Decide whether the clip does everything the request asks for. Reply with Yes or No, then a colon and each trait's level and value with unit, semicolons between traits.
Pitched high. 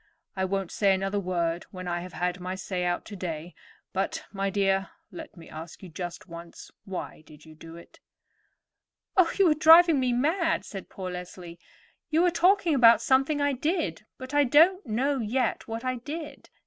Yes: high, 200 Hz